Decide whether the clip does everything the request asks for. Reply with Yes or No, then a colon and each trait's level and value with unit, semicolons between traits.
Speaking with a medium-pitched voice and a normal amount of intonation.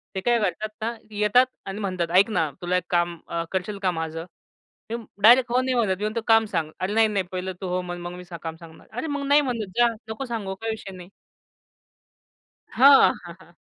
No: high, 200 Hz; average, 4.3 semitones